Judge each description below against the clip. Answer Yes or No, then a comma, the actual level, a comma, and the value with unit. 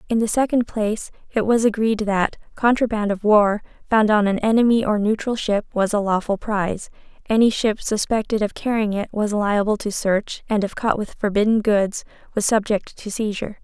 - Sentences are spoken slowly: No, average, 185 wpm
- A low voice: No, high, 210 Hz